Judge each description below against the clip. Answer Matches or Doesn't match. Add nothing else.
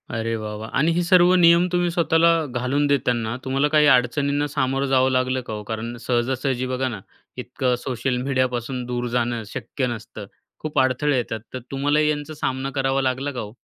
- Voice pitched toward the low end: Matches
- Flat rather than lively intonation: Doesn't match